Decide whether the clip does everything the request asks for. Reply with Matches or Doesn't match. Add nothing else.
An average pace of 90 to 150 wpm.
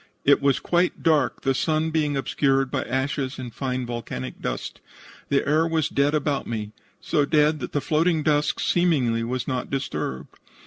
Doesn't match